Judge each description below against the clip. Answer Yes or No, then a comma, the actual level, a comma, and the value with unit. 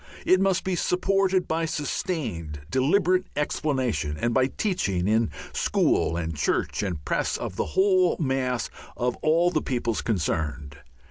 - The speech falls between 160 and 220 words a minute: No, average, 140 wpm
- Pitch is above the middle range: No, low, 130 Hz